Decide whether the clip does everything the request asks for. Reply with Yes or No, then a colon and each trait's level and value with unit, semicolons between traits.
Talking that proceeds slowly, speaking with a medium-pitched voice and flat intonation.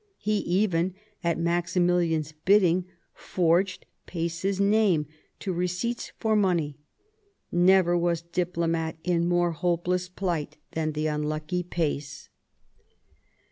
Yes: slow, 100 wpm; medium, 175 Hz; narrow, 1.9 semitones